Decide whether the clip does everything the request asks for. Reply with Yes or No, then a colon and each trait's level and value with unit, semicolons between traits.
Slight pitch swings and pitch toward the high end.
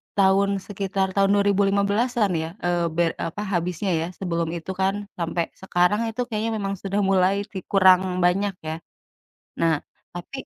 Yes: narrow, 2.3 semitones; high, 195 Hz